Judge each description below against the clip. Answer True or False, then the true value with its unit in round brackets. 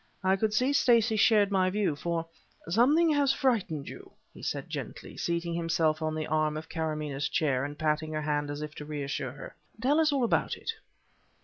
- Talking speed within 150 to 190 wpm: False (200 wpm)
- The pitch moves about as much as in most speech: False (6.4 semitones)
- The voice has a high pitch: False (165 Hz)